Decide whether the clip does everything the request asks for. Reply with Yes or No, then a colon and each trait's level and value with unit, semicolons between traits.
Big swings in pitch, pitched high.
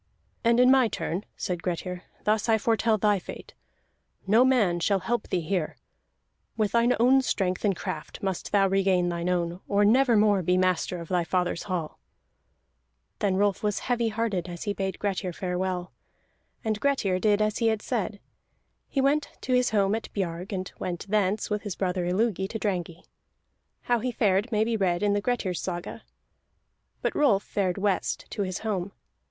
No: average, 3.4 semitones; high, 200 Hz